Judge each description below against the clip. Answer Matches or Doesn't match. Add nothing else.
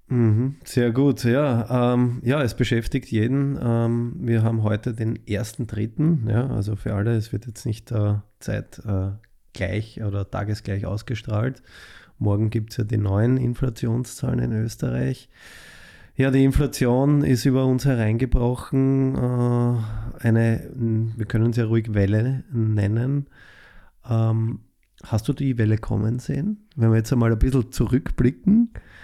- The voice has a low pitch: Matches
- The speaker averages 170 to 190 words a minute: Doesn't match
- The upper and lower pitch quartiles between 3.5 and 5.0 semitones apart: Doesn't match